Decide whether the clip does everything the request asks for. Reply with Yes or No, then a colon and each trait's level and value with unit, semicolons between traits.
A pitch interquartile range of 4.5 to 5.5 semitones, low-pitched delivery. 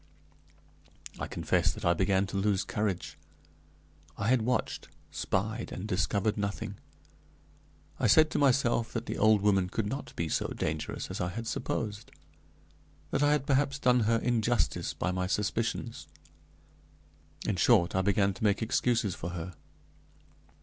No: average, 3.6 semitones; low, 105 Hz